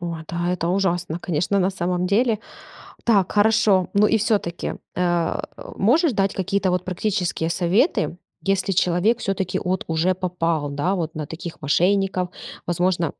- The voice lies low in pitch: No, medium, 180 Hz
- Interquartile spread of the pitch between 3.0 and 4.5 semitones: No, narrow, 2.5 semitones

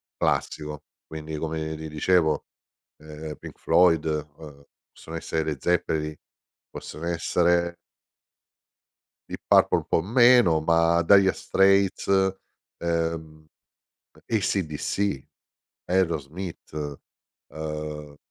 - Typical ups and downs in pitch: No, narrow, 2.2 semitones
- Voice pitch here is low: Yes, very low, 80 Hz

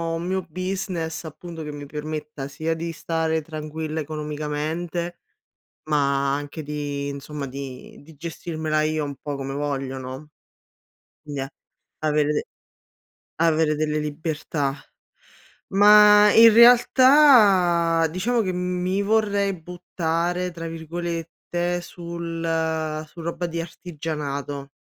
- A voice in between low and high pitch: Yes, medium, 160 Hz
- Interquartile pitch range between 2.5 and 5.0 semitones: Yes, average, 2.8 semitones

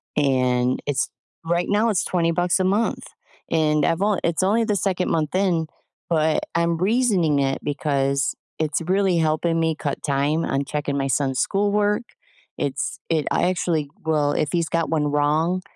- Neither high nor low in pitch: Yes, medium, 160 Hz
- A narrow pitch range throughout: No, average, 4.0 semitones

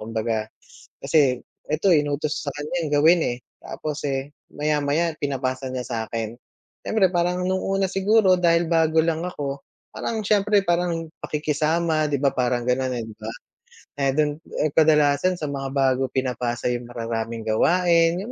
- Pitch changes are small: No, average, 4.6 semitones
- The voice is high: No, medium, 145 Hz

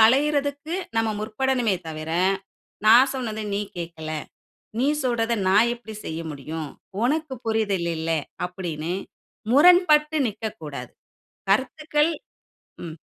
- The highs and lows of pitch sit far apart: Yes, wide, 8.5 semitones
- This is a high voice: Yes, high, 225 Hz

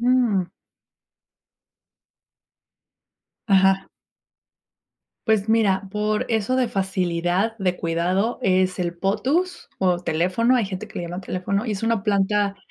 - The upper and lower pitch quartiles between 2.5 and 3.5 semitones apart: Yes, average, 3.1 semitones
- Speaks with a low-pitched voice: No, high, 195 Hz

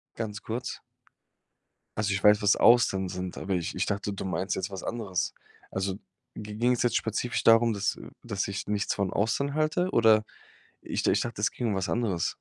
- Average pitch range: Yes, average, 3.3 semitones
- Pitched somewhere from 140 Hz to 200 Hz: No, low, 105 Hz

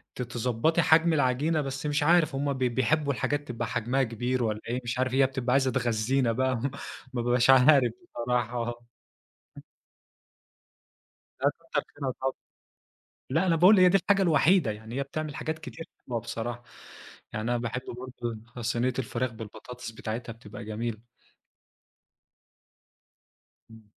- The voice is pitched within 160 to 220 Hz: No, low, 125 Hz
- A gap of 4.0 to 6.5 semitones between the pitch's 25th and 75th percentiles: No, average, 3.5 semitones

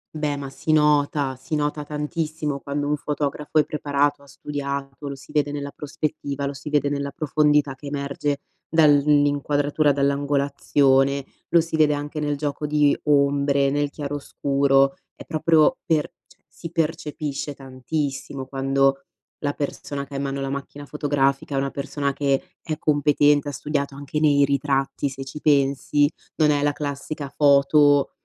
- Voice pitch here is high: No, medium, 145 Hz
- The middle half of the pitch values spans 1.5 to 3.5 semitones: No, narrow, 1.1 semitones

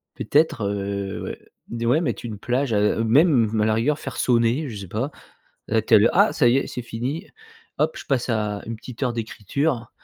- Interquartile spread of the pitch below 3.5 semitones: No, average, 3.9 semitones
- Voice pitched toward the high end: No, low, 115 Hz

